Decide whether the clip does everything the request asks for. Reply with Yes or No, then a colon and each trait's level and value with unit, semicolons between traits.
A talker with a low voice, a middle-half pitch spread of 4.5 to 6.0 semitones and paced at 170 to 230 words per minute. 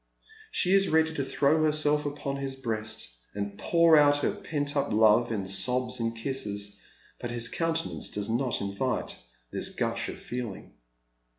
No: low, 130 Hz; average, 5.0 semitones; average, 160 wpm